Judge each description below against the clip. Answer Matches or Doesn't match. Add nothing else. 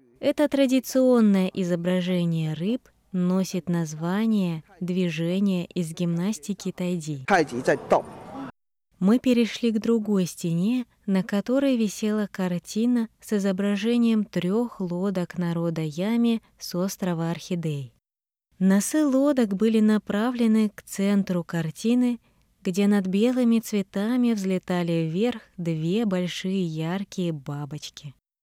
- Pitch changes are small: Doesn't match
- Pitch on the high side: Matches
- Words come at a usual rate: Doesn't match